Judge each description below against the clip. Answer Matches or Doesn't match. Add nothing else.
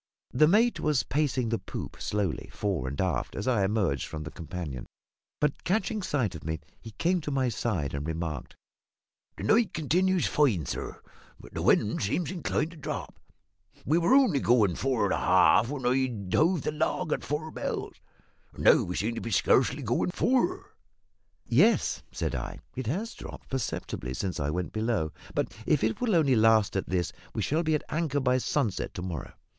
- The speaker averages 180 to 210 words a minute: Matches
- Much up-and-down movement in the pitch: Matches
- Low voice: Matches